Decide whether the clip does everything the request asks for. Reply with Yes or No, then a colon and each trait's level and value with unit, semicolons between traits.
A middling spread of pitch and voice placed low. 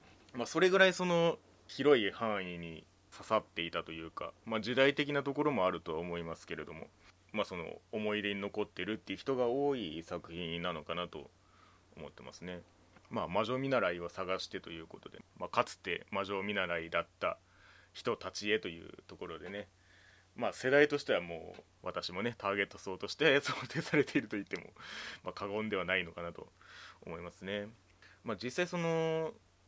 No: wide, 6.5 semitones; low, 100 Hz